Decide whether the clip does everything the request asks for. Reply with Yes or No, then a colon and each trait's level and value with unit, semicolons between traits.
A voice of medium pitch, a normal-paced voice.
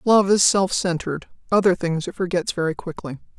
Yes: medium, 180 Hz; average, 175 wpm